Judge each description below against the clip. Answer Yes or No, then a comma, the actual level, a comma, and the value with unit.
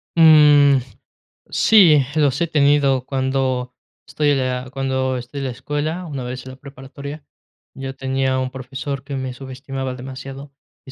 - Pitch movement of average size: No, narrow, 1.7 semitones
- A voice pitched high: No, low, 135 Hz